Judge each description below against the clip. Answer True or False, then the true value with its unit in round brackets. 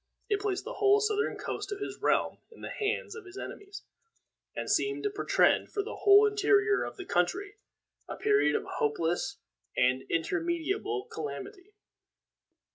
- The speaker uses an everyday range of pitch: False (1.5 semitones)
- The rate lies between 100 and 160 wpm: True (155 wpm)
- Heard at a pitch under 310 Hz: False (410 Hz)